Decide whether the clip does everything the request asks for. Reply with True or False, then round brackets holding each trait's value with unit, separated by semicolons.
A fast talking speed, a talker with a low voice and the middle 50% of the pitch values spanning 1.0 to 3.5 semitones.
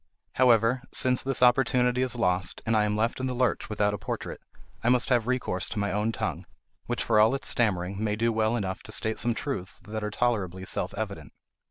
True (215 wpm; 110 Hz; 3.0 semitones)